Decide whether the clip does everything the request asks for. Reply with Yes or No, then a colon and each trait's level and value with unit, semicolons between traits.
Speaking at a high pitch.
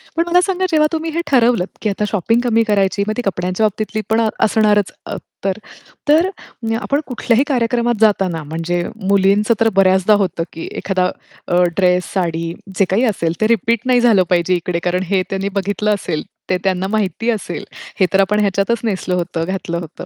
Yes: high, 200 Hz